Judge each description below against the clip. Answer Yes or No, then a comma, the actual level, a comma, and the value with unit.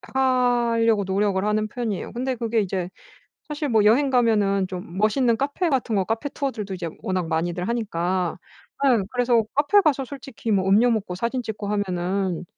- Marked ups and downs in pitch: No, average, 4.5 semitones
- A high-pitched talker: Yes, high, 220 Hz